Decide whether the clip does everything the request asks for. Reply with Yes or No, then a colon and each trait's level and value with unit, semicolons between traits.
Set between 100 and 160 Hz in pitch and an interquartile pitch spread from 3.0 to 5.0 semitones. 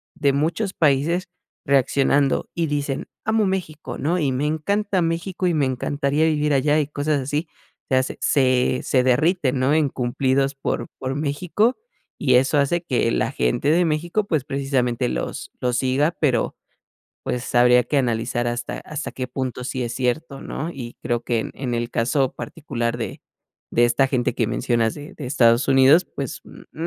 Yes: medium, 140 Hz; average, 3.6 semitones